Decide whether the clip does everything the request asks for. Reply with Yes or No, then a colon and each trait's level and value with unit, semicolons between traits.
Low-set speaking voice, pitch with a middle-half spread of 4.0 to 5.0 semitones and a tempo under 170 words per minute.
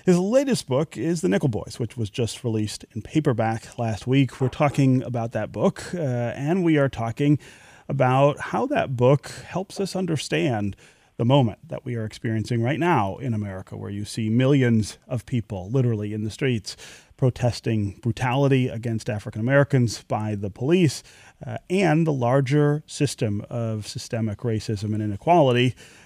Yes: low, 125 Hz; average, 4.5 semitones; average, 160 wpm